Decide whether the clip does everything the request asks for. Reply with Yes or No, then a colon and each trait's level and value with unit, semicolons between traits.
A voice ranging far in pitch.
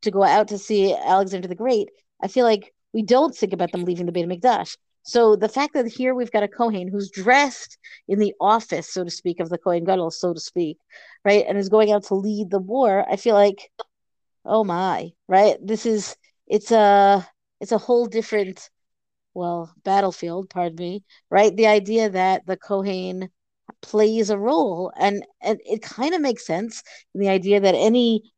No: average, 2.9 semitones